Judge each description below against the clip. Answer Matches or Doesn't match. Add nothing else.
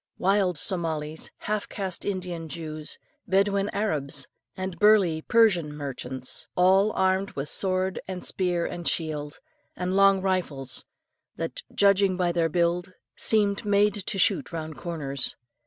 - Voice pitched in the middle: Matches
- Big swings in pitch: Doesn't match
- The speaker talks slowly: Matches